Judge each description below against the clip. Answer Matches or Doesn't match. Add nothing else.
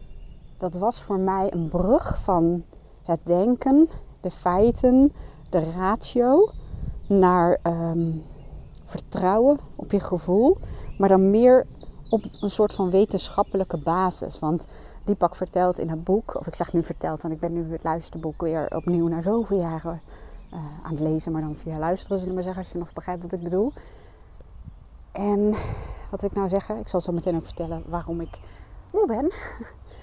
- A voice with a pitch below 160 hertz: Doesn't match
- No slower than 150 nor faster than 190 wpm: Matches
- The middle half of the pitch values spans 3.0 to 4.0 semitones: Matches